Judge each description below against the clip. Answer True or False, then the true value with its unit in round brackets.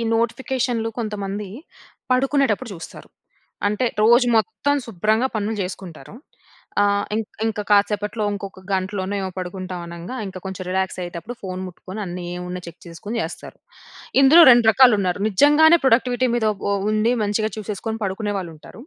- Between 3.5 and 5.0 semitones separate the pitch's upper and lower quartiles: True (3.9 semitones)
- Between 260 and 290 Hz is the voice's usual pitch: False (205 Hz)